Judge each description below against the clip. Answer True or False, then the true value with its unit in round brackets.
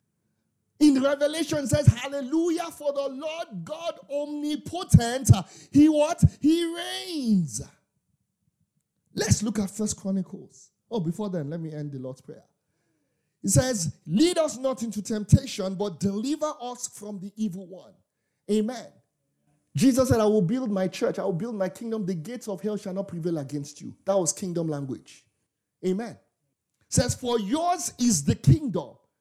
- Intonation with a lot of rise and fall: True (7.1 semitones)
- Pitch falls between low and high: False (215 Hz)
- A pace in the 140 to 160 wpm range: True (155 wpm)